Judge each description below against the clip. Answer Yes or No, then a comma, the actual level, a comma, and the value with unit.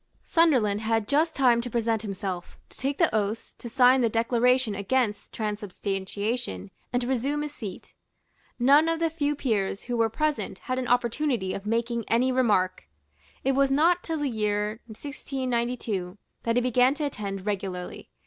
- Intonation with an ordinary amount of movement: Yes, average, 4.4 semitones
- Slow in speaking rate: No, average, 165 wpm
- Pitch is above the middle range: Yes, high, 235 Hz